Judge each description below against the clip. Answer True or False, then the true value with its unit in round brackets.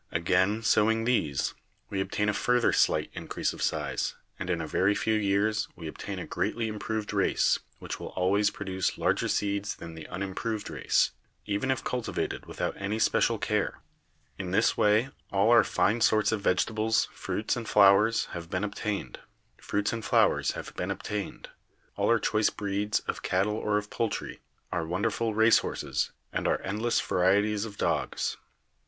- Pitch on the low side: True (105 Hz)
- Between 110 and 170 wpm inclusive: True (155 wpm)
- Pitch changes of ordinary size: False (2.3 semitones)